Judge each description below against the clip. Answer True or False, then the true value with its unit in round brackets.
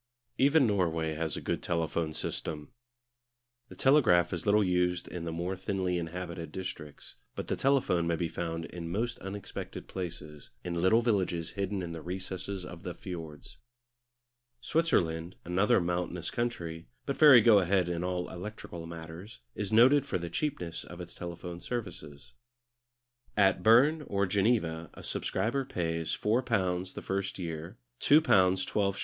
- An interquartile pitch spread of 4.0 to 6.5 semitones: False (3.6 semitones)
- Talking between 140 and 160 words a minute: True (150 wpm)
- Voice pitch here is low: True (90 Hz)